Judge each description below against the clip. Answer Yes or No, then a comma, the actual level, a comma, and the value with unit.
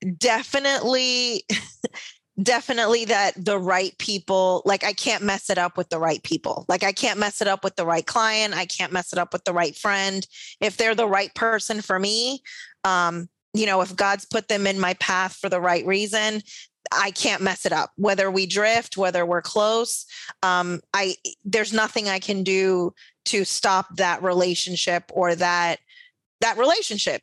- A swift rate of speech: No, average, 180 wpm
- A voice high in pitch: Yes, high, 195 Hz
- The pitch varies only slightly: No, average, 3.1 semitones